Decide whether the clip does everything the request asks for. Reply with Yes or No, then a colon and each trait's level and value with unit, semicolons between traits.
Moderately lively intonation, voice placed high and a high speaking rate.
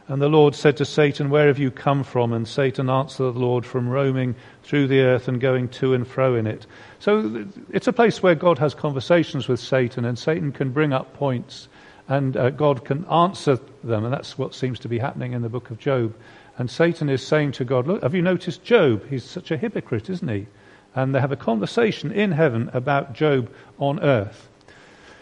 No: average, 3.4 semitones; low, 135 Hz; fast, 210 wpm